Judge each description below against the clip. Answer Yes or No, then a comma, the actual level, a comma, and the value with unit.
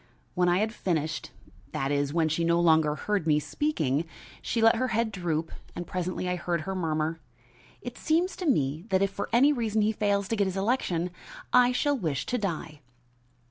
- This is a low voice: No, medium, 180 Hz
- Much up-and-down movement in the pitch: Yes, wide, 5.7 semitones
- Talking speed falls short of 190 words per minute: No, average, 195 wpm